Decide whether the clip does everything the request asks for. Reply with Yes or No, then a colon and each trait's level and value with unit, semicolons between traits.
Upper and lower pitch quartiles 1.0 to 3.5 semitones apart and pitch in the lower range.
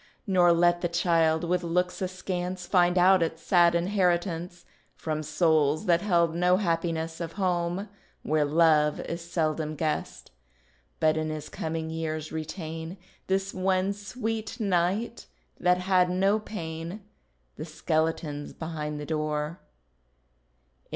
No: narrow, 2.4 semitones; medium, 170 Hz